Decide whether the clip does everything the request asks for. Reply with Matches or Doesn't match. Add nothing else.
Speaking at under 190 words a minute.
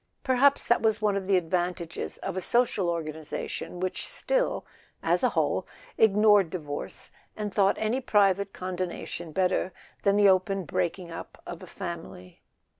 Matches